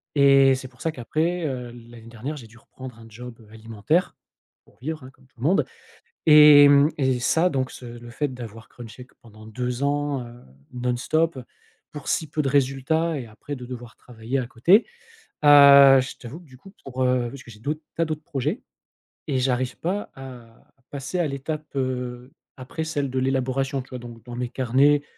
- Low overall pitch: Yes, low, 130 Hz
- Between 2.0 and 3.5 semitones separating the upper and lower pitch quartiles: Yes, average, 3.1 semitones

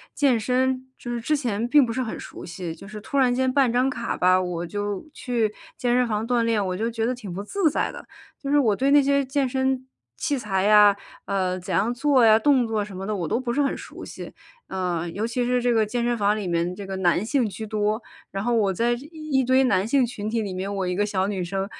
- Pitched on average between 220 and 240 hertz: Yes, high, 225 Hz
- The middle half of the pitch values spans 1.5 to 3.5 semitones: No, average, 4.2 semitones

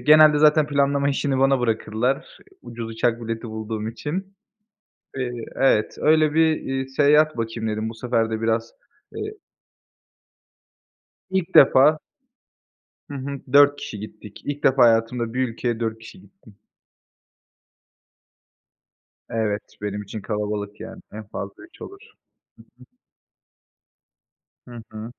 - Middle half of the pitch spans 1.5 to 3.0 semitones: No, average, 4.4 semitones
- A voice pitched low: Yes, low, 120 Hz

